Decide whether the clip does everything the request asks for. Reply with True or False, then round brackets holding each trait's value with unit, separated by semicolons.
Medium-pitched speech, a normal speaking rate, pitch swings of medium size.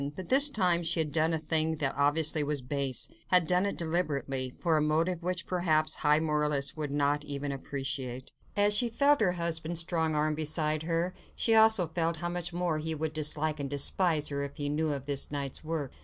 False (155 Hz; 210 wpm; 3.0 semitones)